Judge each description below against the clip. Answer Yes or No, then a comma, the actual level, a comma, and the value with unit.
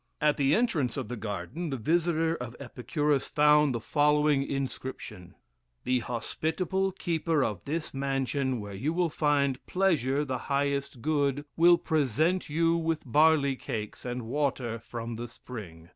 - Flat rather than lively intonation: No, average, 4.2 semitones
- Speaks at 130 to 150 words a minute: Yes, average, 145 wpm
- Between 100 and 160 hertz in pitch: Yes, medium, 140 Hz